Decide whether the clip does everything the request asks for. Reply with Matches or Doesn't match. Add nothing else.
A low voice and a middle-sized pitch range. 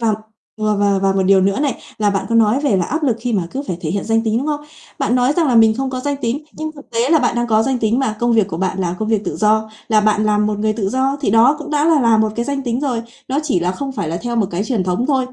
Doesn't match